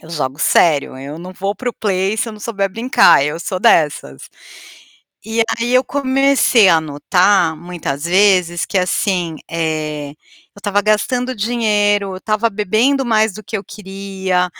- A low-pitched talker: No, high, 195 Hz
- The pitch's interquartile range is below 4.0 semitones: No, average, 4.6 semitones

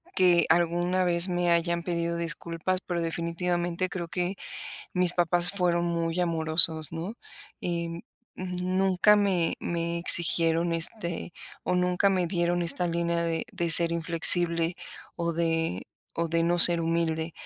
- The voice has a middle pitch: Yes, medium, 170 Hz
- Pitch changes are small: Yes, narrow, 1.1 semitones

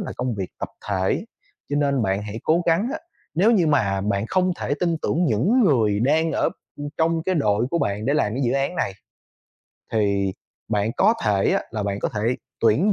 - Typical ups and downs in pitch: No, wide, 7.9 semitones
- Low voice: Yes, low, 125 Hz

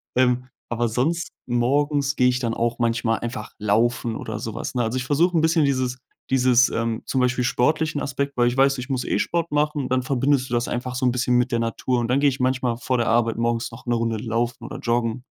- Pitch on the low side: Yes, low, 125 Hz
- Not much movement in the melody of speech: Yes, narrow, 2.2 semitones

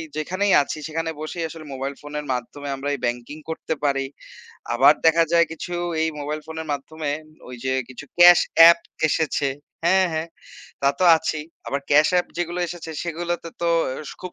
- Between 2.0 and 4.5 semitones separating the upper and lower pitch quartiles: Yes, average, 3.0 semitones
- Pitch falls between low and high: Yes, medium, 160 Hz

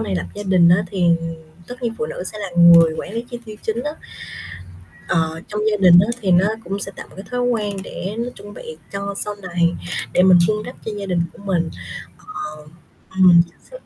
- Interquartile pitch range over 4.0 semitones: No, average, 3.4 semitones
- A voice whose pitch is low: No, high, 195 Hz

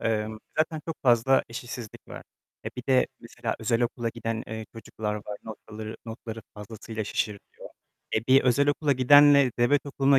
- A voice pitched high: No, low, 115 Hz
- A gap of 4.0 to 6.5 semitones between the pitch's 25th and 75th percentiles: No, average, 3.4 semitones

